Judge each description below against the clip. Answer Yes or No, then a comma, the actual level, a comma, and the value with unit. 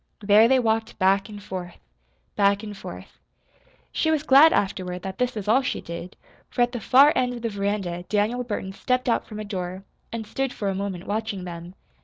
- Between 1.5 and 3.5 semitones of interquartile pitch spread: No, average, 4.1 semitones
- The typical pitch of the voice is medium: No, high, 210 Hz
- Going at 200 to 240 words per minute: Yes, fast, 205 wpm